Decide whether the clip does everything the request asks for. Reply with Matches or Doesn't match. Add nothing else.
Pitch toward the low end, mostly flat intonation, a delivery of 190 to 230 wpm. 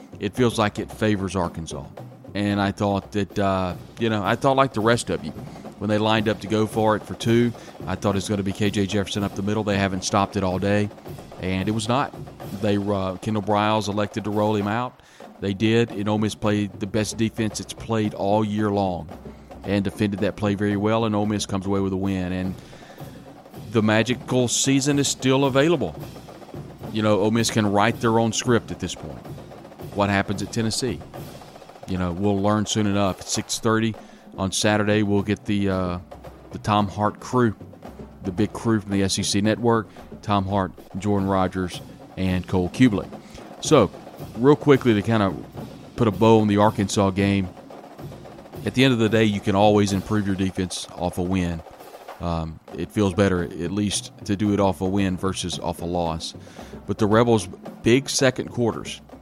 Matches